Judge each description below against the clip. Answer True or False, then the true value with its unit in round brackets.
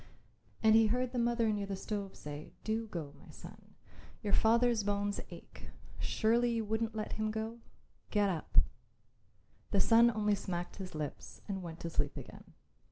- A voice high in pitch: True (215 Hz)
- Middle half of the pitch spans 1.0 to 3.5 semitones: True (2.7 semitones)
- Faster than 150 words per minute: True (165 wpm)